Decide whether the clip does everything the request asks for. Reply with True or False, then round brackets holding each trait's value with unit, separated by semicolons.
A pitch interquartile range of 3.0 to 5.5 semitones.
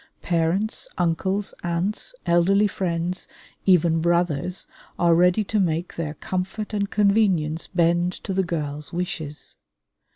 False (2.5 semitones)